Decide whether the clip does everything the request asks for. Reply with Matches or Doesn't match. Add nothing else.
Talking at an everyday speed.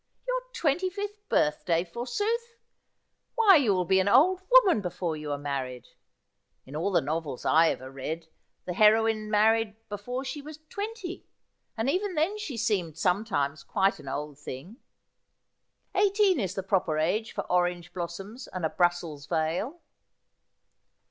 Matches